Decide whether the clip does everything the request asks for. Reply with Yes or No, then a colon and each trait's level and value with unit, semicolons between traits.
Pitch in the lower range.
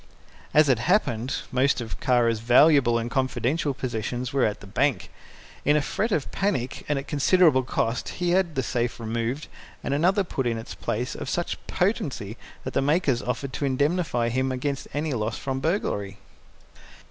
Yes: low, 130 Hz